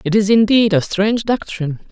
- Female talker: Yes, female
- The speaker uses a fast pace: No, average, 190 wpm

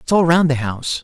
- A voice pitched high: No, medium, 150 Hz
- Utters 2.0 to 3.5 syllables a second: No, 6.1 syllables/s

